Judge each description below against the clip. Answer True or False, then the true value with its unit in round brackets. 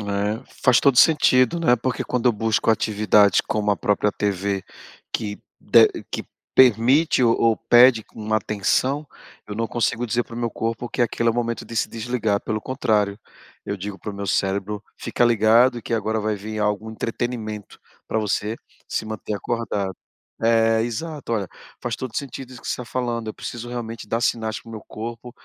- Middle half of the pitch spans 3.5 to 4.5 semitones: False (2.4 semitones)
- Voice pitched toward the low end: True (115 Hz)